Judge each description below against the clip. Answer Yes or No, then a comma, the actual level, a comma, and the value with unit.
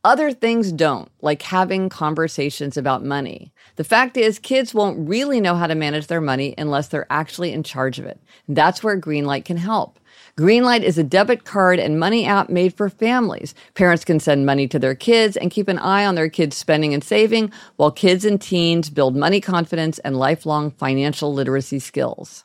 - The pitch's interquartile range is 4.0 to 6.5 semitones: Yes, wide, 5.4 semitones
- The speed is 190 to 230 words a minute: Yes, average, 195 wpm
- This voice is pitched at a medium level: Yes, medium, 165 Hz